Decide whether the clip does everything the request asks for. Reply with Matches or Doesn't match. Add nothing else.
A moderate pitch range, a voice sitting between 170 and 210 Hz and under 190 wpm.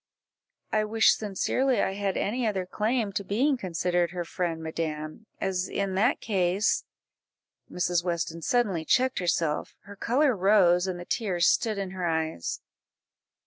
Matches